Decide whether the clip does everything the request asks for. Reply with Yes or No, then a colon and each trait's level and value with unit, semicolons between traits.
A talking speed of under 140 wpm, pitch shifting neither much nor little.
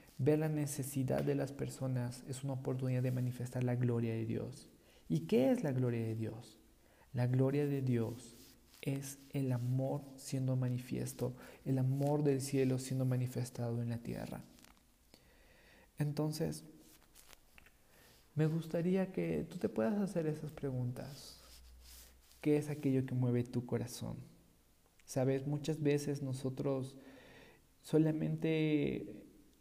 Yes: slow, 125 wpm; average, 3.4 semitones